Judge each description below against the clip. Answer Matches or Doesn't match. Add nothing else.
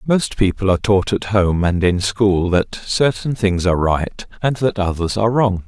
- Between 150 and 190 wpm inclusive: Doesn't match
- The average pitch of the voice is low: Matches